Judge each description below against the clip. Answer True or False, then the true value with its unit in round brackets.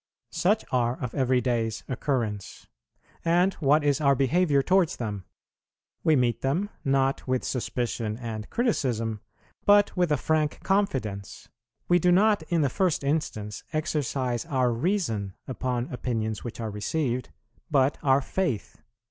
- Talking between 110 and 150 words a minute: True (140 wpm)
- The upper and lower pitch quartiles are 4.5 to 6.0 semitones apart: True (5.4 semitones)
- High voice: False (135 Hz)